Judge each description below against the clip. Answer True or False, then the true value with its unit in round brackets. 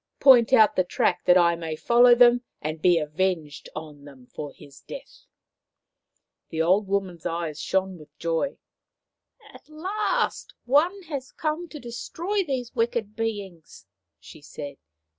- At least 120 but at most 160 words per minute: True (150 wpm)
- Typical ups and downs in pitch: False (8.0 semitones)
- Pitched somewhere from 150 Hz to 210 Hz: True (190 Hz)